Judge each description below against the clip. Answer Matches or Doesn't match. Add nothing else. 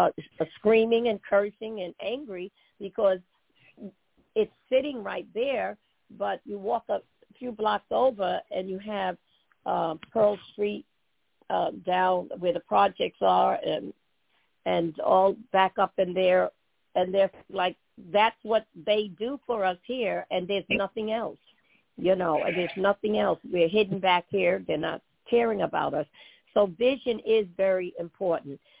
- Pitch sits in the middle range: Doesn't match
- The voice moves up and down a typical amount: Matches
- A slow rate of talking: Doesn't match